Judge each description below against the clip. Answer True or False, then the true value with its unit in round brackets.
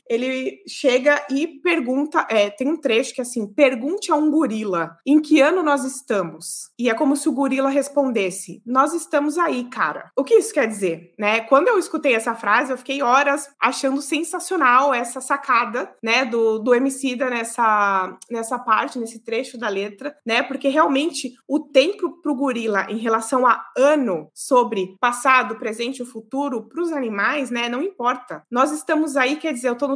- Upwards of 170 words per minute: True (180 wpm)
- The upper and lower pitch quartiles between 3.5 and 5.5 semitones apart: True (4.0 semitones)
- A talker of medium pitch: False (260 Hz)